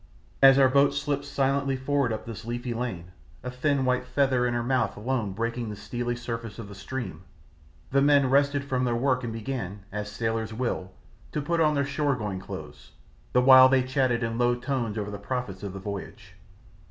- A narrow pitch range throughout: No, average, 3.2 semitones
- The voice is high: No, low, 125 Hz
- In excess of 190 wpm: Yes, average, 200 wpm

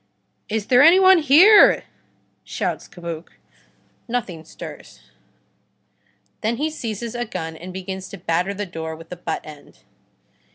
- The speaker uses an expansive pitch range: Yes, wide, 6.6 semitones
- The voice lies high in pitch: Yes, high, 195 Hz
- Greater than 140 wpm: No, slow, 135 wpm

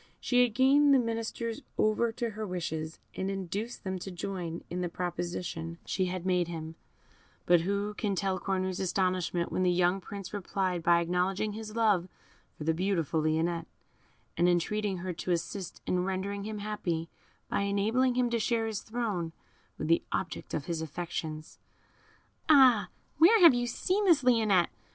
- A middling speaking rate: Yes, average, 170 wpm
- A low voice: No, high, 190 Hz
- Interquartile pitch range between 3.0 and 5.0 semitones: Yes, average, 3.9 semitones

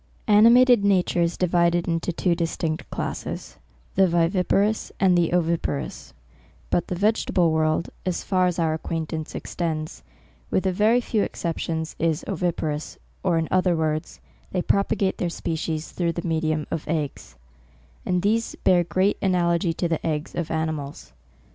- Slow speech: No, average, 155 wpm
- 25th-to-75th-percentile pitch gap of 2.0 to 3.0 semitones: Yes, narrow, 2.5 semitones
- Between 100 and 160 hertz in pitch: No, medium, 170 Hz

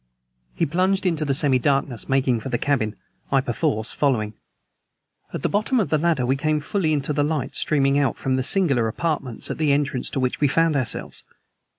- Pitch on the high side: No, medium, 140 Hz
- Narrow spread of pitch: No, average, 3.3 semitones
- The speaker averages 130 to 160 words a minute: No, average, 200 wpm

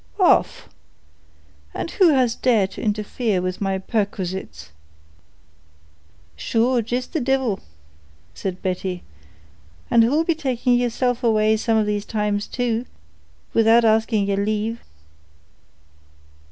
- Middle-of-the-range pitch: No, high, 225 Hz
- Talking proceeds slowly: Yes, slow, 115 wpm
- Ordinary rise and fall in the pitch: Yes, average, 3.4 semitones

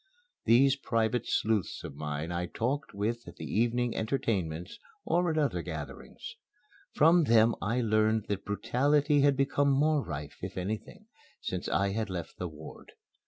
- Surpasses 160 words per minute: No, average, 155 wpm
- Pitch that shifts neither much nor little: No, wide, 7.0 semitones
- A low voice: Yes, low, 110 Hz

